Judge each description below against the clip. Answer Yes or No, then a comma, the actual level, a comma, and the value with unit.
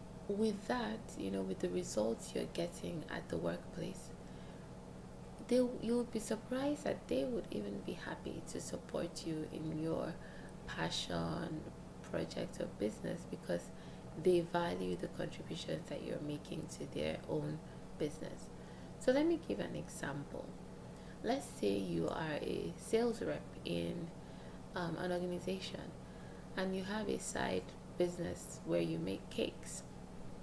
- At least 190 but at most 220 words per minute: No, average, 140 wpm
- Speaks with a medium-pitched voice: Yes, medium, 175 Hz